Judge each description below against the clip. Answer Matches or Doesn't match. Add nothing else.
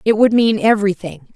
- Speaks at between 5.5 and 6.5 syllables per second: Matches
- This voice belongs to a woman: Matches